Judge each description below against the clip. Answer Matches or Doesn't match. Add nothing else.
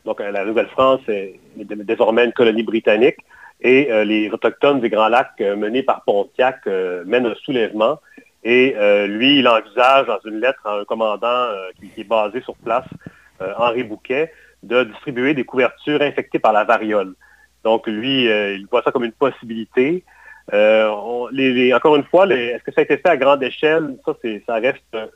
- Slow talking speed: Doesn't match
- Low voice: Matches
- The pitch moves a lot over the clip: Doesn't match